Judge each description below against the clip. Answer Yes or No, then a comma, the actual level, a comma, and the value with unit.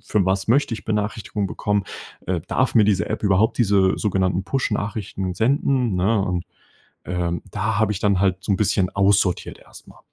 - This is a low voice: Yes, low, 100 Hz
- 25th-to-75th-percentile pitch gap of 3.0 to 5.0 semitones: No, narrow, 2.4 semitones